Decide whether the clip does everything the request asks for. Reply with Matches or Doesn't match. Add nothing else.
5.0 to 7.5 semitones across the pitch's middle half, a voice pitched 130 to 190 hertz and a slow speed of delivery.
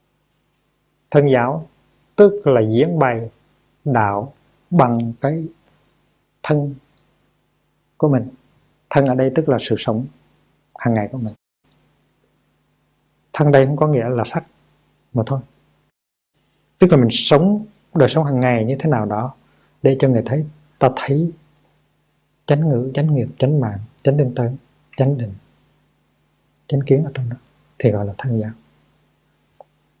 Doesn't match